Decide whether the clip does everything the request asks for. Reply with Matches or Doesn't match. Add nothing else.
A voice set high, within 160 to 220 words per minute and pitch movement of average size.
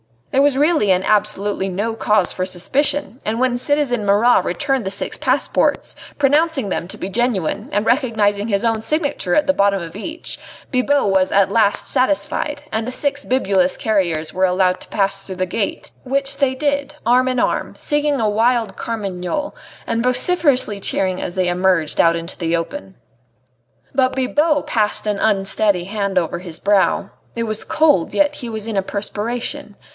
Doesn't match